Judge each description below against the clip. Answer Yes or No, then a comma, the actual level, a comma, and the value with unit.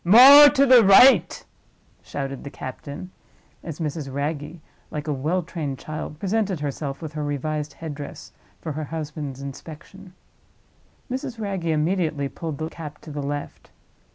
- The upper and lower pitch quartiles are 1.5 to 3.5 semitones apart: No, average, 4.0 semitones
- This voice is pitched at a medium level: Yes, medium, 155 Hz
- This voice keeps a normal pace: Yes, average, 150 wpm